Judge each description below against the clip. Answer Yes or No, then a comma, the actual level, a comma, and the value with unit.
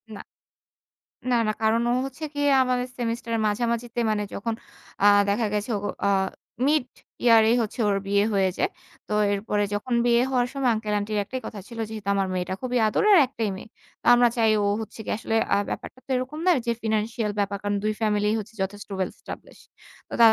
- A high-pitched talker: Yes, high, 225 Hz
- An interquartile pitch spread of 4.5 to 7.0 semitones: No, average, 2.9 semitones